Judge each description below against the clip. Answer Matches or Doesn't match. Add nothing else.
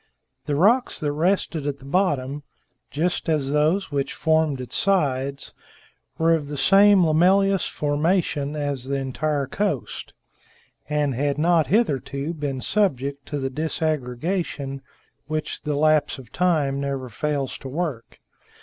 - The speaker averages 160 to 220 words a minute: Doesn't match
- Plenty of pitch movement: Doesn't match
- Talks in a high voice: Doesn't match